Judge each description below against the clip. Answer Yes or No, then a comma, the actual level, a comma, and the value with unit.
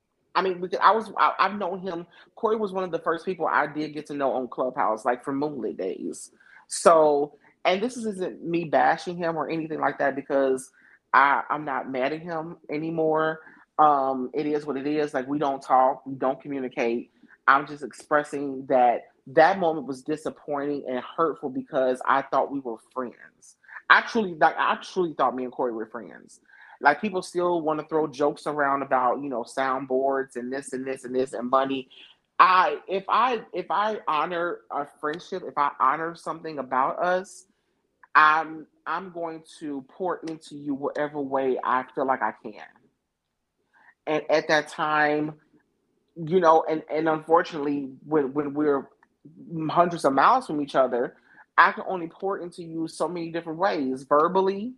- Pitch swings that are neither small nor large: Yes, average, 3.7 semitones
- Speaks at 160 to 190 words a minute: Yes, average, 175 wpm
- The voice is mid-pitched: Yes, medium, 150 Hz